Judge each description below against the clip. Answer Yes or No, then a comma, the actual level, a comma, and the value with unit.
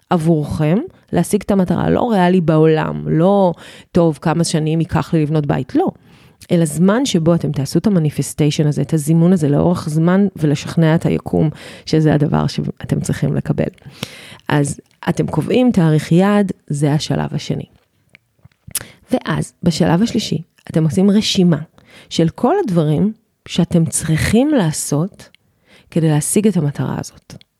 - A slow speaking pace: No, average, 135 wpm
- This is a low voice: No, medium, 165 Hz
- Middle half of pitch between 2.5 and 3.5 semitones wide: Yes, average, 3.2 semitones